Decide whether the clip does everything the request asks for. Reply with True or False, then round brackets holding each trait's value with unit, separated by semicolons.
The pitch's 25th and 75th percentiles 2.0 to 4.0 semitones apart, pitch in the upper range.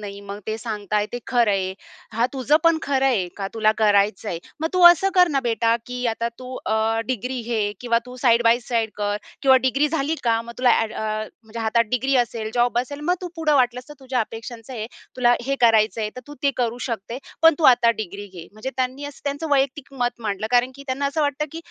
True (3.7 semitones; 240 Hz)